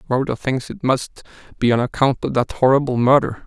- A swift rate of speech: No, average, 190 wpm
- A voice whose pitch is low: Yes, low, 130 Hz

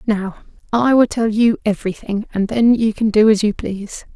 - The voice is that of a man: No, female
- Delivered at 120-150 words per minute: No, average, 200 wpm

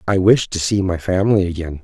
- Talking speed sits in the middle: No, fast, 230 wpm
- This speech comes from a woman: No, male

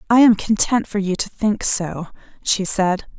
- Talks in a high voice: Yes, high, 200 Hz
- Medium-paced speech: Yes, average, 190 wpm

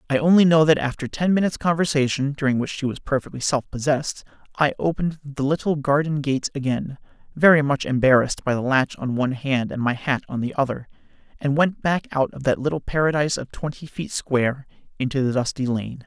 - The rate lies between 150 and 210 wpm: Yes, average, 200 wpm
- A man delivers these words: Yes, male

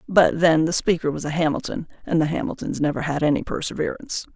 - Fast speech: No, average, 195 wpm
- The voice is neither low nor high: Yes, medium, 160 Hz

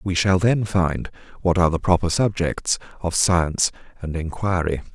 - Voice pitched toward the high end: No, very low, 90 Hz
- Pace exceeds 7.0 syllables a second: No, 4.8 syllables/s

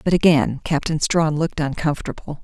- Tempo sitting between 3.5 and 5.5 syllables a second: No, 5.7 syllables/s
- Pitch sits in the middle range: Yes, medium, 155 Hz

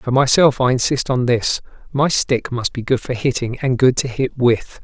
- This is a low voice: Yes, low, 125 Hz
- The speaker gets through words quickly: Yes, fast, 210 wpm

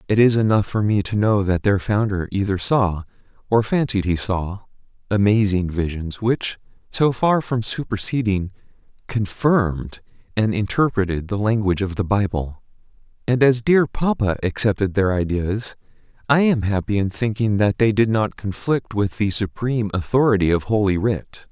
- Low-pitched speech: Yes, low, 105 Hz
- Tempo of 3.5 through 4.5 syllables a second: No, 4.8 syllables/s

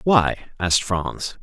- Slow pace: Yes, slow, 125 wpm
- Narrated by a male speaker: Yes, male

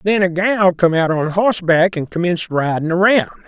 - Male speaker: Yes, male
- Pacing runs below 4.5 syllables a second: No, 5.0 syllables/s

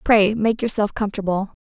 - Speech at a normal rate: Yes, average, 150 wpm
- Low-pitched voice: No, high, 210 Hz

